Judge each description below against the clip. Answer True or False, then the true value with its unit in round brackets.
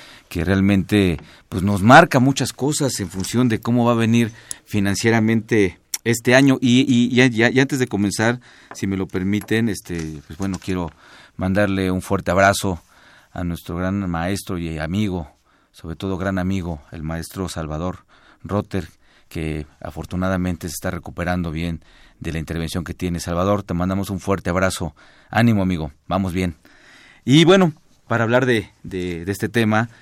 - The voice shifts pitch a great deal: False (4.7 semitones)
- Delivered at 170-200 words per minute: False (160 wpm)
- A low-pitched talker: True (95 Hz)